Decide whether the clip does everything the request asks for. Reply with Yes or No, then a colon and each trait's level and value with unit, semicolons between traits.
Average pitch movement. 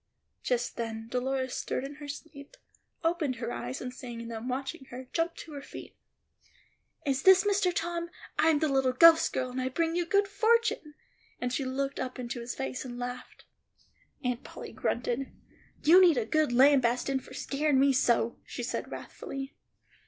Yes: average, 4.4 semitones